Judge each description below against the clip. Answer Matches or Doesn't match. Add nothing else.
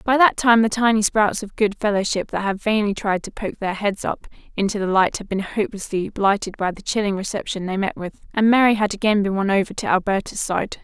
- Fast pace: Matches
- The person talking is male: Doesn't match